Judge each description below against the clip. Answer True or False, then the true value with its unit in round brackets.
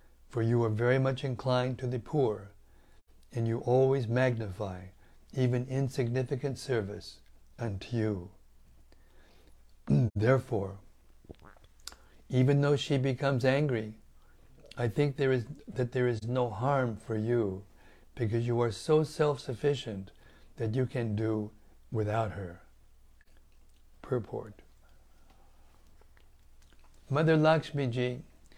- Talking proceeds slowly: True (105 wpm)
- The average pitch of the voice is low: True (115 Hz)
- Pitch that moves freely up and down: True (6.3 semitones)